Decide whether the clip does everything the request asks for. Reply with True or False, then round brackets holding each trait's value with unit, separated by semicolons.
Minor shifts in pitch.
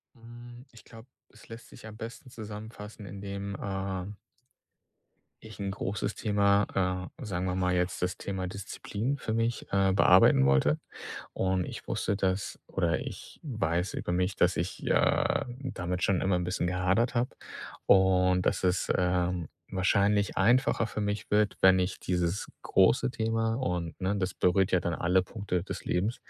False (3.0 semitones)